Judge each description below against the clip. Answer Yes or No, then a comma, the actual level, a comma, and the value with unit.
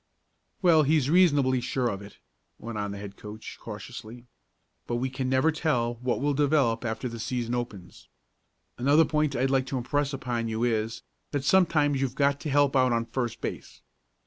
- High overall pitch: No, low, 130 Hz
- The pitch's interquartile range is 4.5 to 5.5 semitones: No, average, 3.6 semitones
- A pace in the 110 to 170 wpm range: No, average, 180 wpm